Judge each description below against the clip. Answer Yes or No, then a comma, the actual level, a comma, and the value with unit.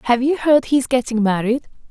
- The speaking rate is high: Yes, fast, 220 wpm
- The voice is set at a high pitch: Yes, very high, 250 Hz